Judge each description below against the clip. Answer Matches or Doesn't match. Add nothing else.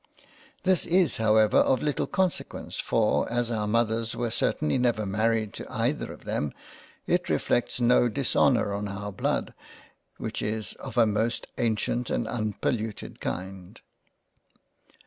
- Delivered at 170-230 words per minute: Doesn't match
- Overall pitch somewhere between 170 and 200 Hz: Doesn't match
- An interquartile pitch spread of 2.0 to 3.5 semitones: Matches